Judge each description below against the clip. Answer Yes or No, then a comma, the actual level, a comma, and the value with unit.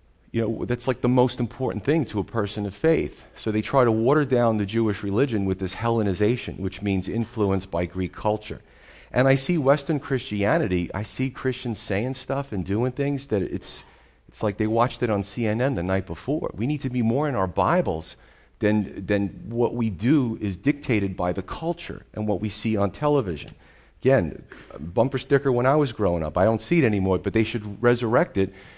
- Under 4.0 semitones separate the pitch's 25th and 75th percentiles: No, average, 4.6 semitones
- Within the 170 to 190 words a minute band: No, fast, 205 wpm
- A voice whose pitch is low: Yes, low, 110 Hz